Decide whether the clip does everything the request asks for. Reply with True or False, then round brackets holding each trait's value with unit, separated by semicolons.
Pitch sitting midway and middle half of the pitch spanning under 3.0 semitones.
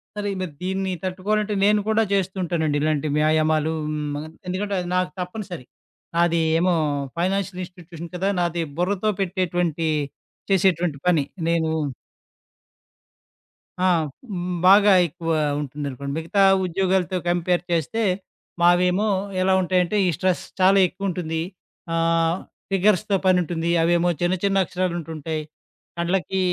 True (180 Hz; 2.5 semitones)